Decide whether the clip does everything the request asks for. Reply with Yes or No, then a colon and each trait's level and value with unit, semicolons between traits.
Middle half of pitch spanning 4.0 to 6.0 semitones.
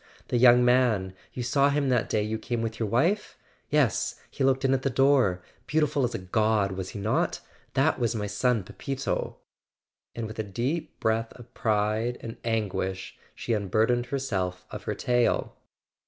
No: average, 3.5 semitones